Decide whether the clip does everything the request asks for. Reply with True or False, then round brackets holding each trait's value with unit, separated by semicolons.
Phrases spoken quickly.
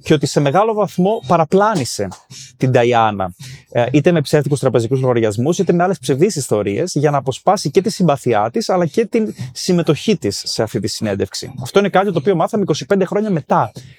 True (185 wpm)